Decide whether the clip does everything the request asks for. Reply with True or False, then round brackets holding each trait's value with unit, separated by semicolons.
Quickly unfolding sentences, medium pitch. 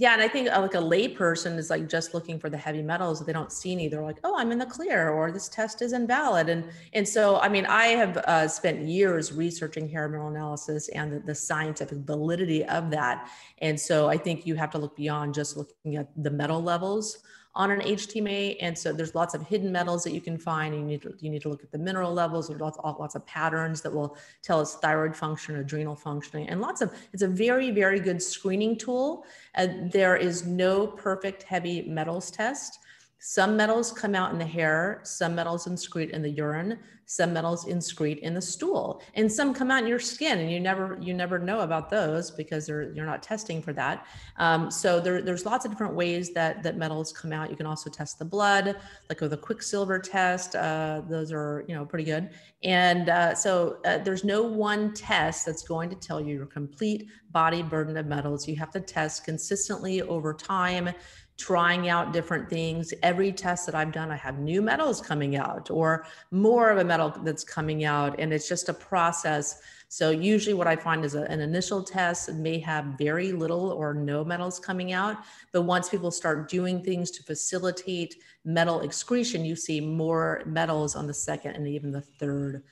True (215 wpm; 170 Hz)